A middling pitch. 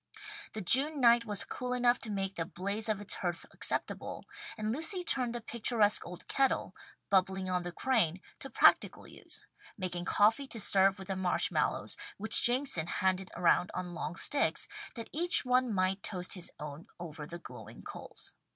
No: high, 200 Hz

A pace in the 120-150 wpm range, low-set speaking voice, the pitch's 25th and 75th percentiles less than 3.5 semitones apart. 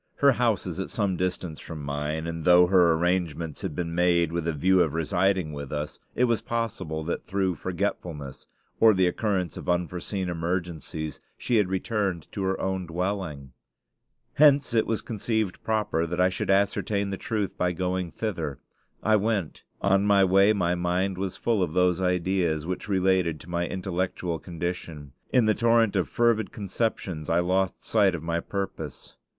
No: average, 175 wpm; very low, 90 Hz; average, 2.9 semitones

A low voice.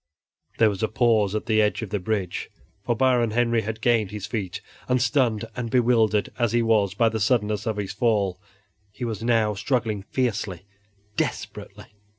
Yes: low, 110 Hz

